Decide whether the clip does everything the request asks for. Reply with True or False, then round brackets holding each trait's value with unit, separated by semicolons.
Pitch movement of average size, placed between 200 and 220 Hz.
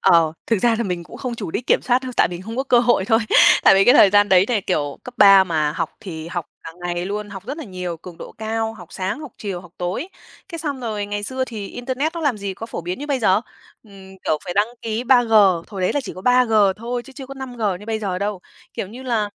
True (4.7 semitones; 210 Hz)